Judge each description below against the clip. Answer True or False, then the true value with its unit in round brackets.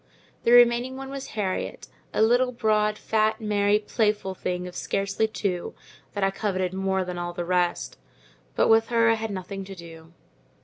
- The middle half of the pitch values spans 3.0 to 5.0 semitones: True (3.6 semitones)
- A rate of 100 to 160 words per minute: False (170 wpm)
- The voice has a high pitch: True (200 Hz)